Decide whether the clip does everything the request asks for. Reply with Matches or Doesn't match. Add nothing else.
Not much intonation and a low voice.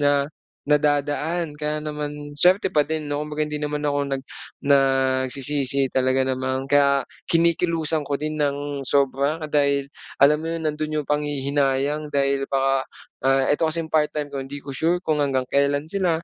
Doesn't match